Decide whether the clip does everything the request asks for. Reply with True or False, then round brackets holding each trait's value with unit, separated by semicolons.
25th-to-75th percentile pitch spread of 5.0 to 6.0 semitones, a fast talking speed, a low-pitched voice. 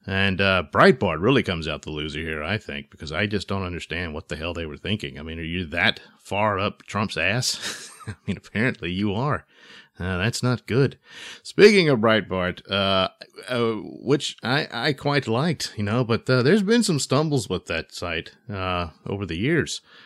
False (5.5 semitones; 195 wpm; 100 Hz)